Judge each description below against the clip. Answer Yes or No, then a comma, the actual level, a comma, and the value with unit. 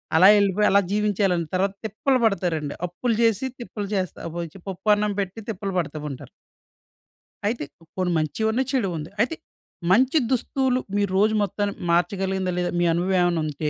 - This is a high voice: Yes, high, 195 Hz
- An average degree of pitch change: Yes, average, 3.4 semitones